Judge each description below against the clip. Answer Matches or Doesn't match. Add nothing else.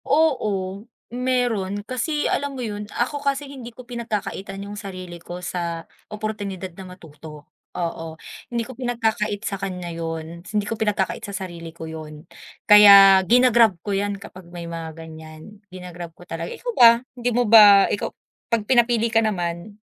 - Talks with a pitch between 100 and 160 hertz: Doesn't match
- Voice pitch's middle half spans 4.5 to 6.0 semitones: Matches